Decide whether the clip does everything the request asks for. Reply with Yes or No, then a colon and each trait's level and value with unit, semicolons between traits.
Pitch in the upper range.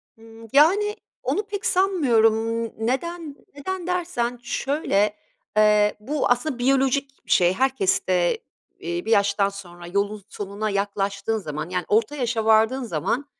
Yes: high, 225 Hz